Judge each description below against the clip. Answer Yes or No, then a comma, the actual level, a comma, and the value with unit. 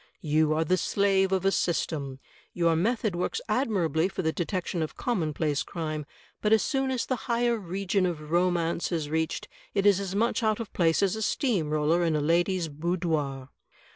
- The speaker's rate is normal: Yes, average, 190 wpm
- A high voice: No, medium, 175 Hz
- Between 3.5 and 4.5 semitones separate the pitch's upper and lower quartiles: Yes, average, 4.1 semitones